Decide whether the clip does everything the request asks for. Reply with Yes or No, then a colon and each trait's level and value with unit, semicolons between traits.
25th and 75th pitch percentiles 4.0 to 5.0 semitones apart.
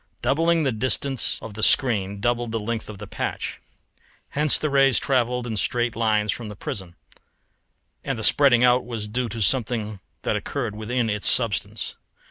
No: average, 3.3 semitones